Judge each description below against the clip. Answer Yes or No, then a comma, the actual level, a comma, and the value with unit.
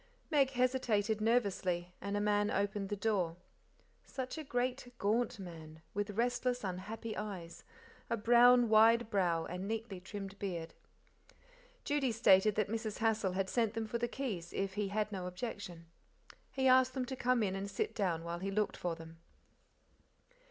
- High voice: Yes, high, 210 Hz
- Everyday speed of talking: Yes, average, 165 wpm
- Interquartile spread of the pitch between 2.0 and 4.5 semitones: Yes, average, 3.9 semitones